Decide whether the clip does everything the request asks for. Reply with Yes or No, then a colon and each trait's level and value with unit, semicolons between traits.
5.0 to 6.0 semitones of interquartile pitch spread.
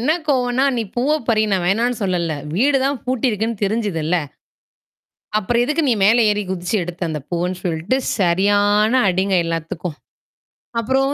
Yes: wide, 5.4 semitones